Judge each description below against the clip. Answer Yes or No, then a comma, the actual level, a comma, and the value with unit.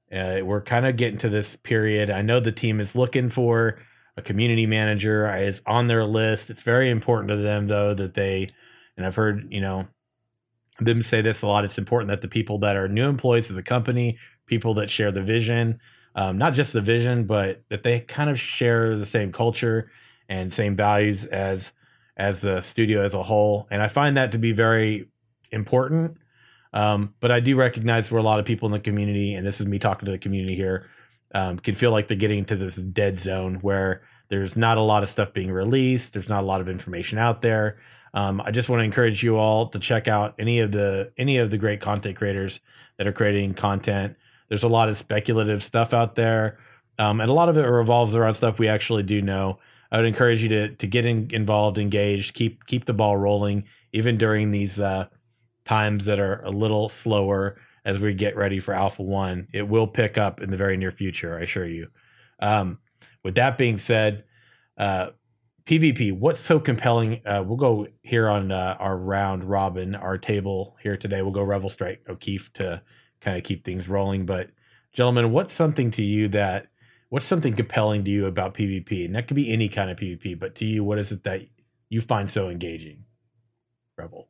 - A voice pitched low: Yes, low, 105 Hz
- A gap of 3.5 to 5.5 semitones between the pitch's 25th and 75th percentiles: No, average, 2.8 semitones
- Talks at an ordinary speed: No, fast, 210 wpm